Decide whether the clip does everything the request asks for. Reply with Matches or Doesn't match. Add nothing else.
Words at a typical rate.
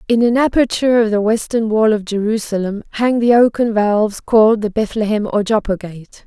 Matches